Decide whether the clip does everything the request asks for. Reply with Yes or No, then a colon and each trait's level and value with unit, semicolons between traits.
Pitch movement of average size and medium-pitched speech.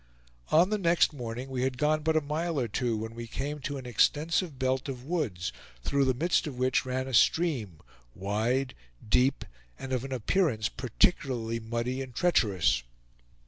No: average, 4.4 semitones; low, 130 Hz